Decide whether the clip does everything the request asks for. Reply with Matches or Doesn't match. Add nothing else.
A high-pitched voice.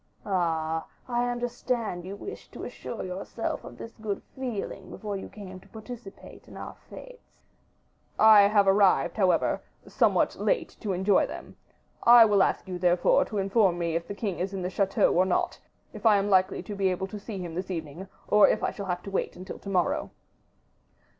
Matches